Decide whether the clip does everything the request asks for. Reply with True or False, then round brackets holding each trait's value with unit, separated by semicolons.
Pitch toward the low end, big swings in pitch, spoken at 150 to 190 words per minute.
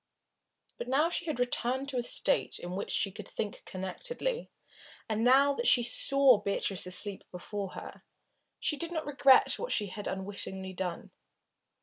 False (235 Hz; 6.4 semitones; 165 wpm)